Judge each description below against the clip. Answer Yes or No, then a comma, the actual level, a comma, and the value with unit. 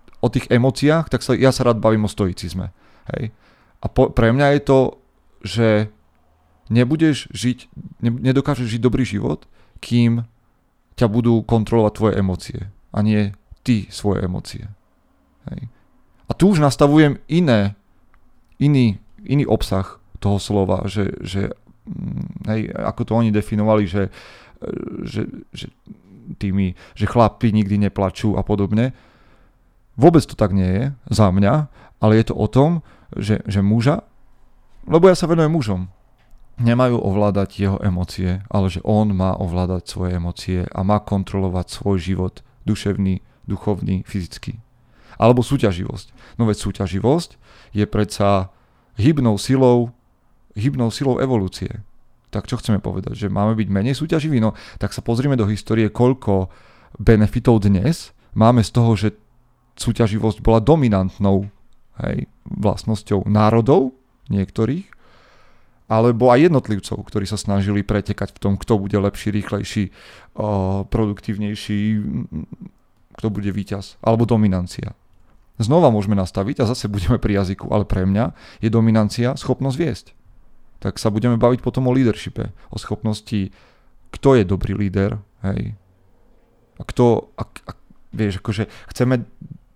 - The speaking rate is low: No, average, 130 wpm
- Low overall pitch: Yes, low, 110 Hz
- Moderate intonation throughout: Yes, average, 3.5 semitones